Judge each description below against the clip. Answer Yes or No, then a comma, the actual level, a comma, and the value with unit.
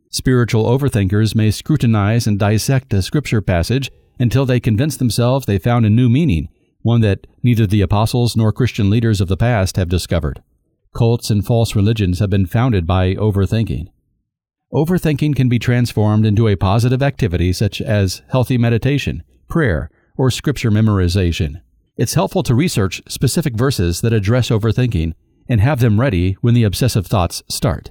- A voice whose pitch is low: Yes, low, 115 Hz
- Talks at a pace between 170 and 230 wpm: No, average, 160 wpm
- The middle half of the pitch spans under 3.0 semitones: No, average, 3.7 semitones